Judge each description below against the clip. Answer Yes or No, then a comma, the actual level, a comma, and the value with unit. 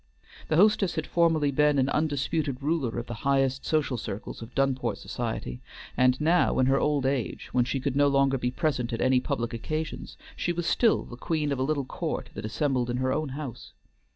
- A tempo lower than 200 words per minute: No, fast, 205 wpm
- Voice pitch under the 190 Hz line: Yes, low, 135 Hz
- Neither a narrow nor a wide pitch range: Yes, average, 3.3 semitones